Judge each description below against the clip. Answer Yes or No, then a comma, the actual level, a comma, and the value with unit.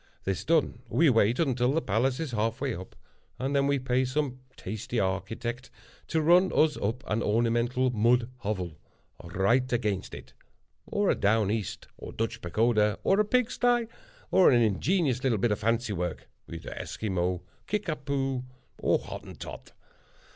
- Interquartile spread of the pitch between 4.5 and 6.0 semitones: Yes, average, 4.8 semitones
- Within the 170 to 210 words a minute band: No, average, 155 wpm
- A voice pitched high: No, low, 120 Hz